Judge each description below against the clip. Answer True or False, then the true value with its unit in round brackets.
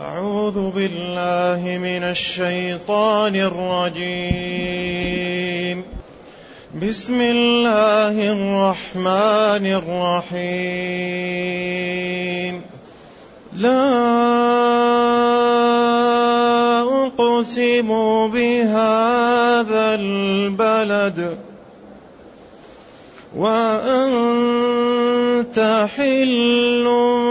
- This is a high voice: True (215 Hz)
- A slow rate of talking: True (35 wpm)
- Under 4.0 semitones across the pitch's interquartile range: False (4.9 semitones)